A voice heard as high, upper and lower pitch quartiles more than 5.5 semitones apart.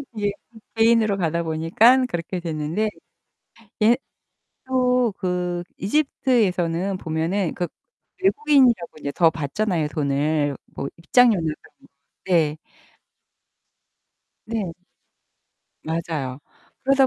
No: medium, 180 Hz; wide, 5.9 semitones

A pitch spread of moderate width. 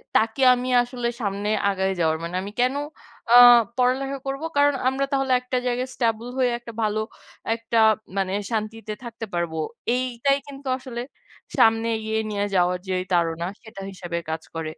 Yes: average, 4.8 semitones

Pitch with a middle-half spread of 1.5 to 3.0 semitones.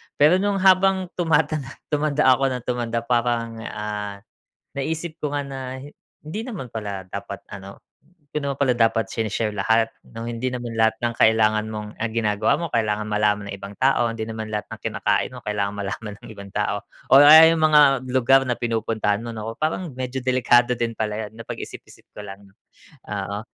No: average, 4.4 semitones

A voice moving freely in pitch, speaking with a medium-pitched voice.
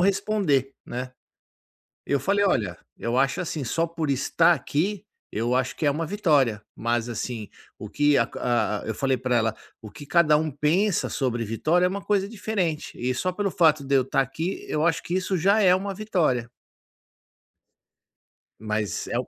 Yes: wide, 6.6 semitones; medium, 150 Hz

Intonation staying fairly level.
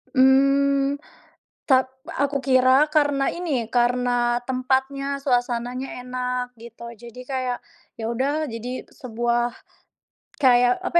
Yes: narrow, 2.1 semitones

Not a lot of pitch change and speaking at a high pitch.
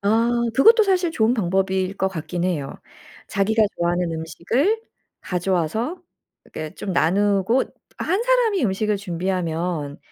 No: wide, 5.4 semitones; high, 195 Hz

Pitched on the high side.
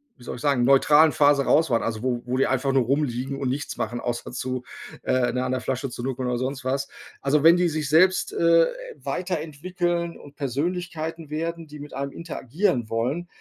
No: medium, 140 Hz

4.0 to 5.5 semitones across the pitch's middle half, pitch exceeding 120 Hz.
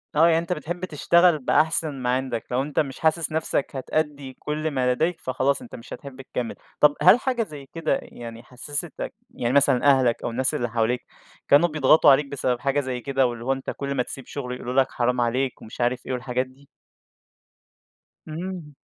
No: average, 3.5 semitones; low, 135 Hz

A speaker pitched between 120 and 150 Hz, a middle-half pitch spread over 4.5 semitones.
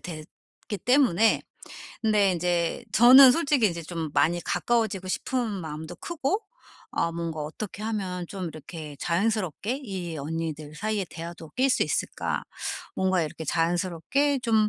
No: medium, 185 Hz; average, 5.3 semitones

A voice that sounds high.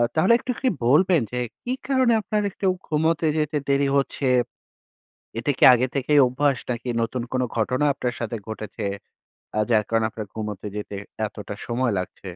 No: low, 130 Hz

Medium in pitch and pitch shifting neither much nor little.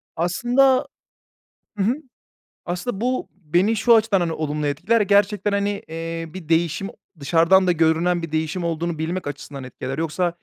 Yes: medium, 175 Hz; average, 4.0 semitones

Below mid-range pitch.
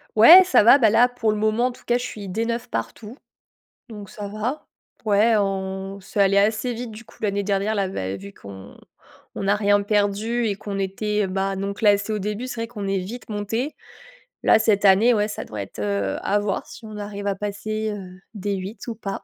No: high, 205 Hz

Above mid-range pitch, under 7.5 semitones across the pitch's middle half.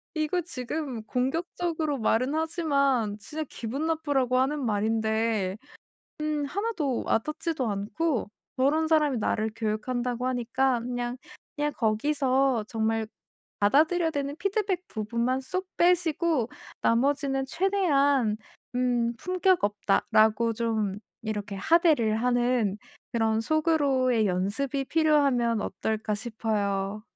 Yes: very high, 255 Hz; wide, 5.6 semitones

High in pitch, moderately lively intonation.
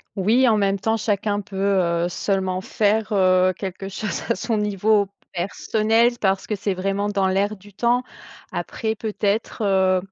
No: high, 200 Hz; narrow, 2.1 semitones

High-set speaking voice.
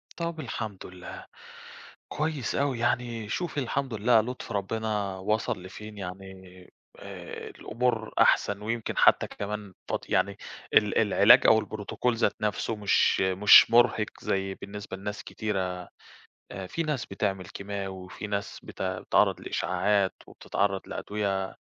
No: low, 105 Hz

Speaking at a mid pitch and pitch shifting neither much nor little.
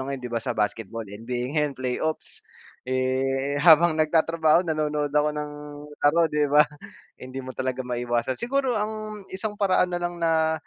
Yes: medium, 150 Hz; average, 4.4 semitones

